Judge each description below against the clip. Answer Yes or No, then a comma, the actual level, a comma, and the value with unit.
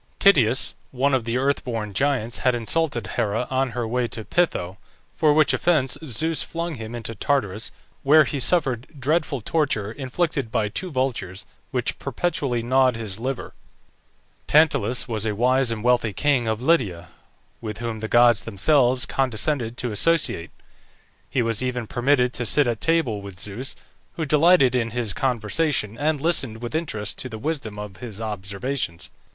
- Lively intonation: No, average, 4.3 semitones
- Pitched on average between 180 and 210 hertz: No, low, 125 Hz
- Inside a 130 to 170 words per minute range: Yes, average, 160 wpm